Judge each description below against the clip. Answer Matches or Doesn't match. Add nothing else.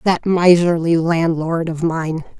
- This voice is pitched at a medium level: Matches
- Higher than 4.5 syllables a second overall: Doesn't match